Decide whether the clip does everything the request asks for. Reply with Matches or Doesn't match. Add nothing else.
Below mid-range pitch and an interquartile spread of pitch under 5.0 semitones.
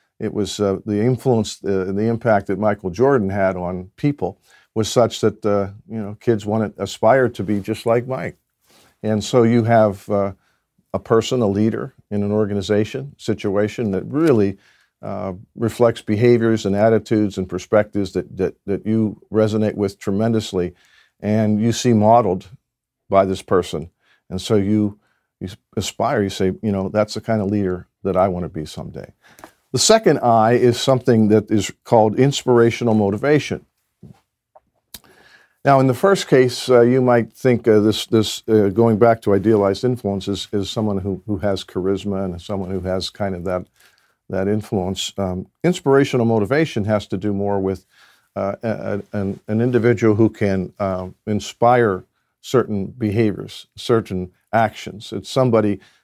Matches